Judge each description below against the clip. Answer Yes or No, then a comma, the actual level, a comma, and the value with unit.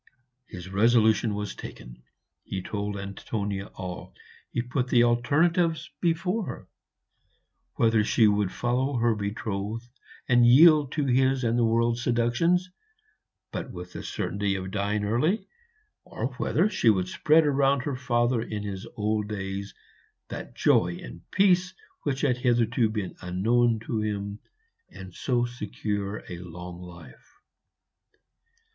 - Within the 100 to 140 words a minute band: Yes, slow, 135 wpm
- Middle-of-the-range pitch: No, low, 115 Hz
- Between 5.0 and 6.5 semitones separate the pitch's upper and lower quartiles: No, average, 4.2 semitones